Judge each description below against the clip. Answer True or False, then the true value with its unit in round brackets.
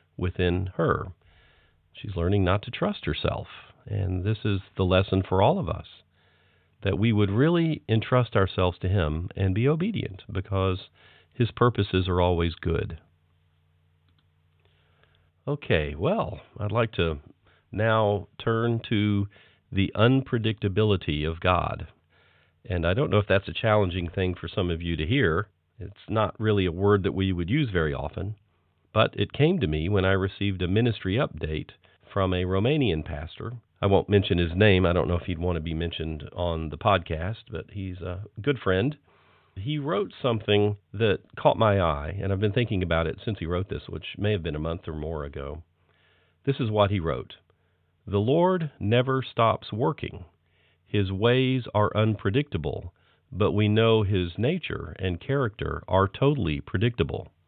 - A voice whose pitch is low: True (95 Hz)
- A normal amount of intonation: True (4.0 semitones)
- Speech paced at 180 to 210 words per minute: False (165 wpm)